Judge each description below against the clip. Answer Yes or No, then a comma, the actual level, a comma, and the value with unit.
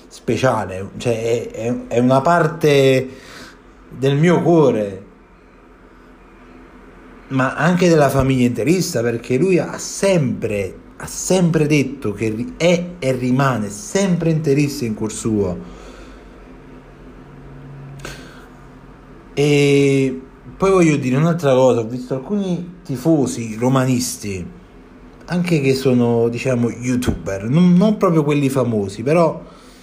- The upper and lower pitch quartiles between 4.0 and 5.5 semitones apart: Yes, average, 5.1 semitones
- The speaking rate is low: Yes, slow, 105 wpm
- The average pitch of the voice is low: Yes, low, 130 Hz